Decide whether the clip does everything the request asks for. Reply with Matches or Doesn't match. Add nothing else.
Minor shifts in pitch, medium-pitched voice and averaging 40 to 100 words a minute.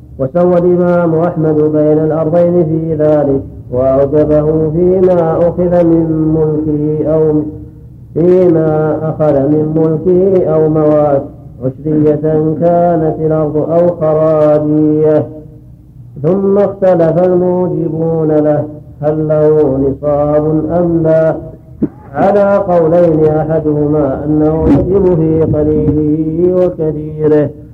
Matches